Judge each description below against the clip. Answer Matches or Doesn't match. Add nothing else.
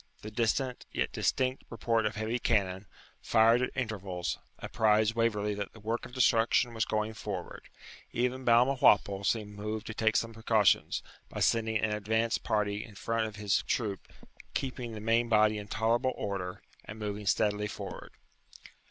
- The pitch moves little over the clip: Matches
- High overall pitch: Doesn't match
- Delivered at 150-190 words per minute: Matches